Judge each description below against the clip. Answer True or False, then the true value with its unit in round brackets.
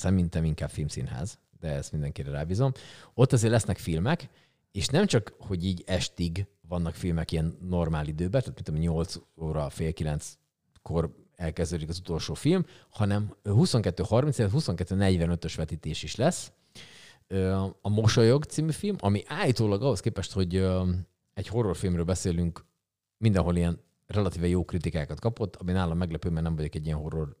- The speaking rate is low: False (140 wpm)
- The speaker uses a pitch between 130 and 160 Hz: False (90 Hz)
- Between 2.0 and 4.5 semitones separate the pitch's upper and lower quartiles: False (5.0 semitones)